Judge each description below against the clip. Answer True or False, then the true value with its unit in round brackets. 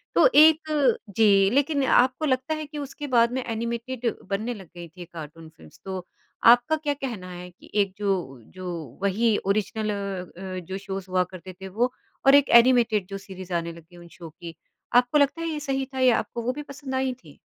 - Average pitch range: False (6.1 semitones)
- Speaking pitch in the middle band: False (230 Hz)